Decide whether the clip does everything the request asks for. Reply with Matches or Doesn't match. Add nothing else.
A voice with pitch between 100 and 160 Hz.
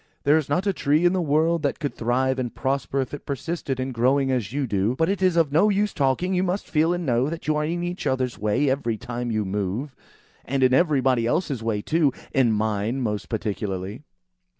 Matches